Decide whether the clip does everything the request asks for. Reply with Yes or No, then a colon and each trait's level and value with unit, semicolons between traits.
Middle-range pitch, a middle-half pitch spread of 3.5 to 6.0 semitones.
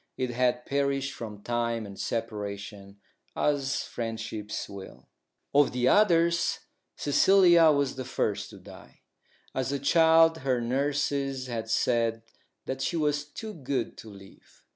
No: low, 130 Hz; average, 4.3 semitones